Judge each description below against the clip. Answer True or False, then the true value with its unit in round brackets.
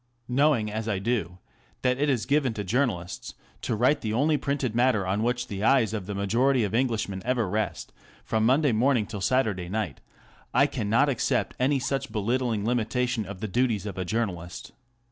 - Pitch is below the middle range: True (115 Hz)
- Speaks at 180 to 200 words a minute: True (185 wpm)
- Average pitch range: True (3.8 semitones)